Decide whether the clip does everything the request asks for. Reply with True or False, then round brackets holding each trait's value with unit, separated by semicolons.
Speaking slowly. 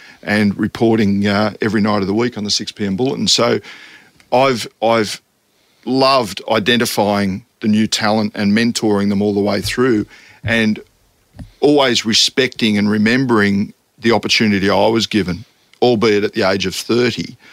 False (150 wpm)